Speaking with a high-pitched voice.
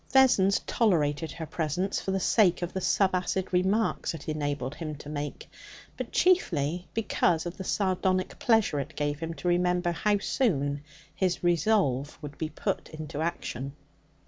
No: medium, 175 Hz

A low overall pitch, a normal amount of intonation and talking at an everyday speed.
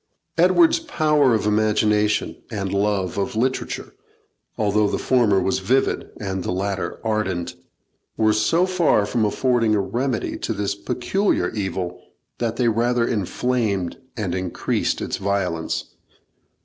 No: low, 105 Hz; average, 3.8 semitones; slow, 130 wpm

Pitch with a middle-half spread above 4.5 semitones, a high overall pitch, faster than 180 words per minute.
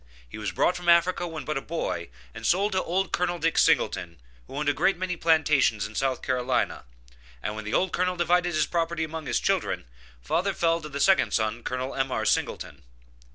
No: wide, 5.5 semitones; medium, 160 Hz; average, 200 wpm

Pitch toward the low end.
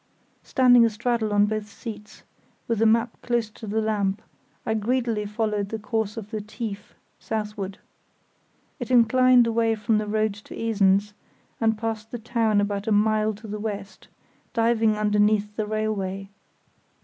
No: high, 215 Hz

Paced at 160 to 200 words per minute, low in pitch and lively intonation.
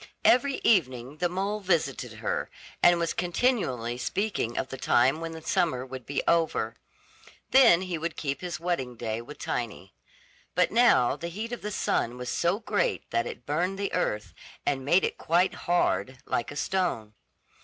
No: average, 175 wpm; medium, 165 Hz; wide, 6.7 semitones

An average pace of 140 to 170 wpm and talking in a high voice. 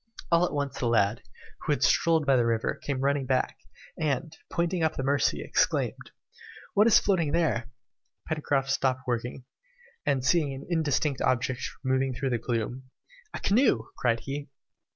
No: average, 160 wpm; low, 135 Hz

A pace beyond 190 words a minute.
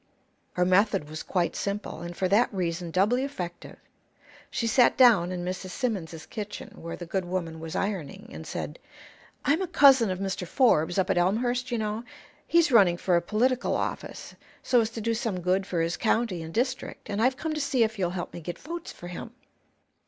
Yes: average, 200 wpm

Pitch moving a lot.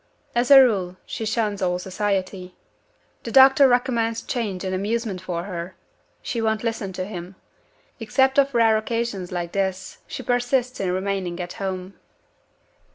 No: average, 4.1 semitones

